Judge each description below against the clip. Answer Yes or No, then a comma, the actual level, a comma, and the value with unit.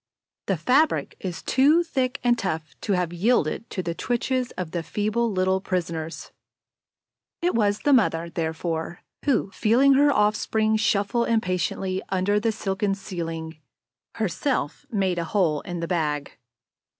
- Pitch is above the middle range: Yes, high, 195 Hz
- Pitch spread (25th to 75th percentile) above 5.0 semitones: Yes, wide, 5.4 semitones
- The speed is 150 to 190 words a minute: No, average, 140 wpm